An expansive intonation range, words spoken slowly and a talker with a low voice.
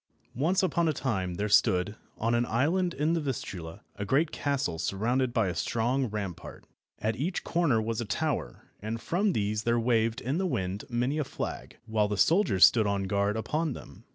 No: wide, 5.9 semitones; average, 190 wpm; low, 115 Hz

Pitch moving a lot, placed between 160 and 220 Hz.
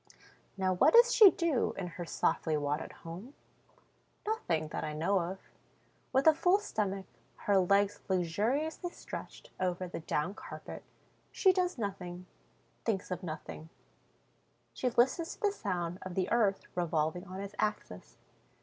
Yes: wide, 6.6 semitones; high, 190 Hz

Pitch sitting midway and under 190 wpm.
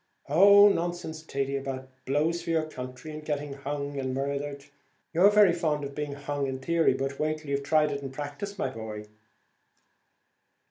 Yes: medium, 145 Hz; average, 175 wpm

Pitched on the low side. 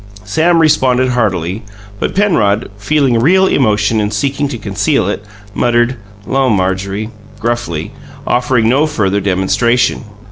Yes: low, 115 Hz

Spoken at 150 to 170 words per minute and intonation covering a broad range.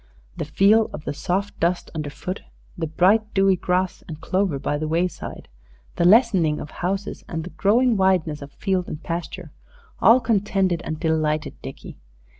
No: average, 160 wpm; average, 3.7 semitones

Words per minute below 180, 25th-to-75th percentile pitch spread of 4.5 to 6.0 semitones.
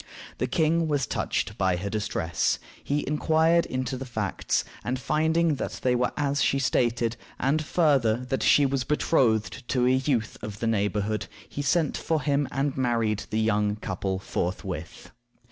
Yes: average, 160 wpm; average, 5.0 semitones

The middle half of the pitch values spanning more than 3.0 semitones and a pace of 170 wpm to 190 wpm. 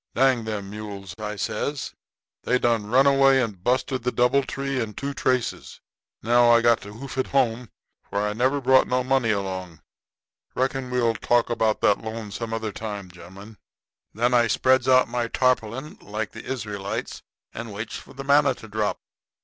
Yes: average, 3.5 semitones; average, 175 wpm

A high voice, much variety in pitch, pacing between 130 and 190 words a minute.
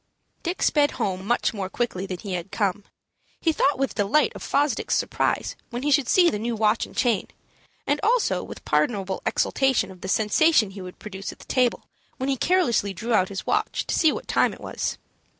No: high, 220 Hz; wide, 6.0 semitones; fast, 205 wpm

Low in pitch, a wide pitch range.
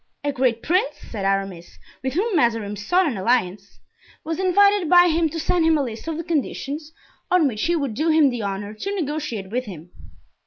No: very high, 280 Hz; wide, 7.6 semitones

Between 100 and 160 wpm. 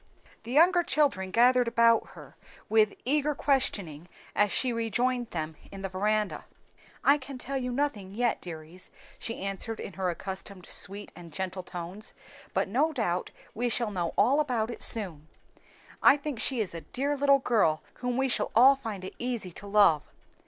No: average, 175 wpm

